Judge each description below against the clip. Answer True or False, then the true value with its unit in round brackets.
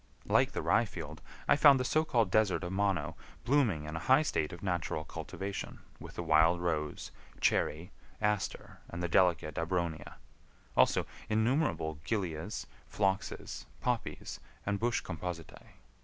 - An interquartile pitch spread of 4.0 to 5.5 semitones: True (5.0 semitones)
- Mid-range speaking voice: False (90 Hz)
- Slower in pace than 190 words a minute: True (140 wpm)